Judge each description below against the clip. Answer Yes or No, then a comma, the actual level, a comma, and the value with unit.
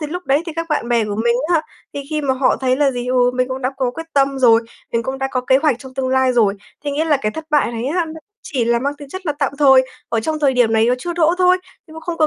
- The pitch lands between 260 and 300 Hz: Yes, very high, 270 Hz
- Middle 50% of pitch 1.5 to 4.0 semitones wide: Yes, average, 3.6 semitones